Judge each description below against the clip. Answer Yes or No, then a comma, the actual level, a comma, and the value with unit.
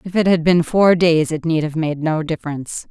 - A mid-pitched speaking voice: Yes, medium, 165 Hz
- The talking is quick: Yes, fast, 250 wpm